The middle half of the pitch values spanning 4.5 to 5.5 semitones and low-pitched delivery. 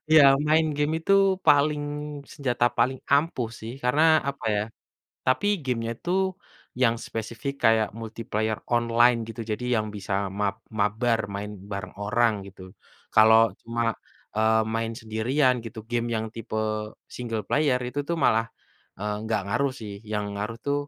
No: average, 4.0 semitones; low, 115 Hz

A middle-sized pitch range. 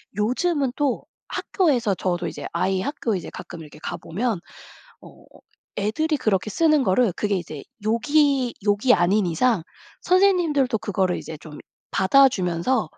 No: wide, 6.9 semitones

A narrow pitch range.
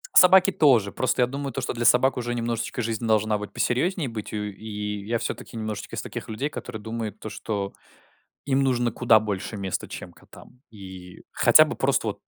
No: average, 3.2 semitones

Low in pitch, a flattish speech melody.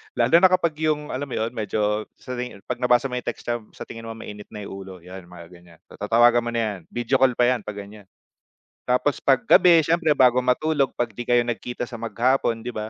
No: low, 120 Hz; average, 3.4 semitones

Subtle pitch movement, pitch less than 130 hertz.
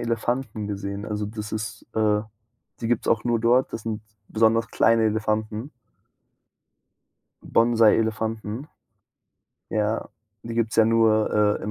Yes: narrow, 1.3 semitones; low, 110 Hz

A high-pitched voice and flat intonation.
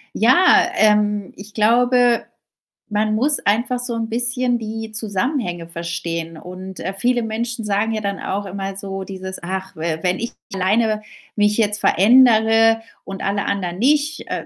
No: high, 210 Hz; average, 3.5 semitones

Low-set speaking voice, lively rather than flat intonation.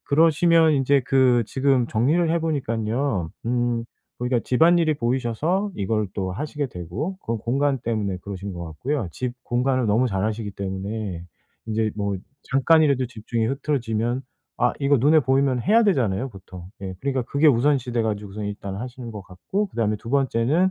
No: low, 120 Hz; average, 4.8 semitones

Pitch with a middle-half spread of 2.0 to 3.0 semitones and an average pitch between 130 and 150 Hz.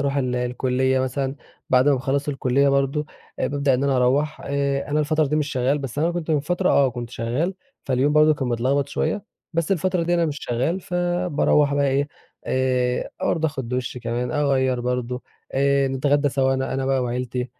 Yes: average, 2.7 semitones; medium, 140 Hz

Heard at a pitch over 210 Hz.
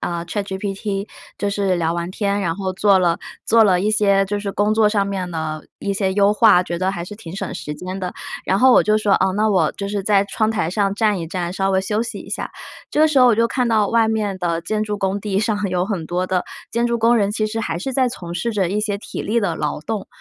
No: high, 200 Hz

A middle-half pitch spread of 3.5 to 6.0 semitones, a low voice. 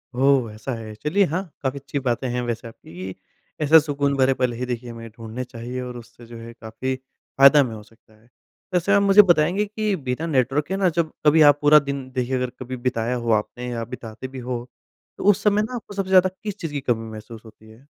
Yes: average, 4.5 semitones; low, 130 Hz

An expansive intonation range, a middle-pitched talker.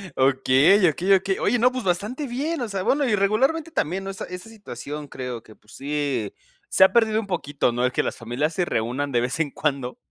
Yes: wide, 8.3 semitones; medium, 175 Hz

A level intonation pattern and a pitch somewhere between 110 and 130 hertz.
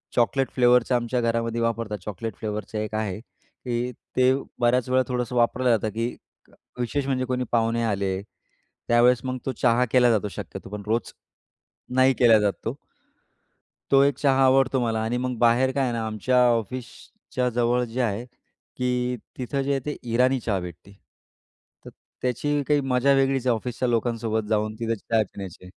Yes: narrow, 2.3 semitones; low, 120 Hz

